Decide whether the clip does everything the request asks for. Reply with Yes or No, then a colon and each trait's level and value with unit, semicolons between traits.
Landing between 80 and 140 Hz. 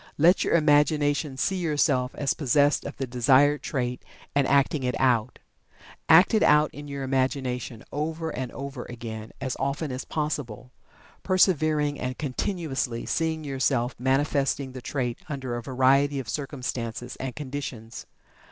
Yes: low, 135 Hz